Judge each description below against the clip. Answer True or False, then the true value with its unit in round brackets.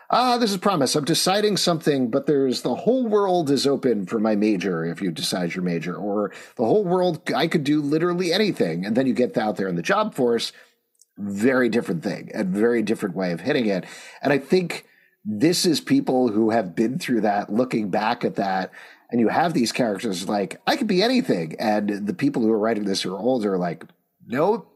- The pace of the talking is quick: True (220 wpm)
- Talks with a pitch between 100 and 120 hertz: False (135 Hz)